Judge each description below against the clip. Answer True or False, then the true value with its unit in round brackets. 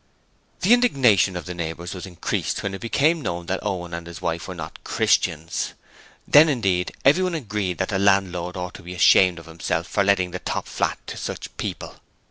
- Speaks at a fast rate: False (195 wpm)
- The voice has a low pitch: True (95 Hz)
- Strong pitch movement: False (3.4 semitones)